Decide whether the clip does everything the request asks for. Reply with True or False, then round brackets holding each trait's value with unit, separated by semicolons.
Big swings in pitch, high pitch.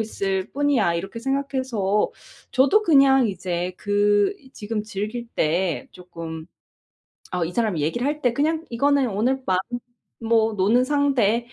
True (5.8 semitones; 225 Hz)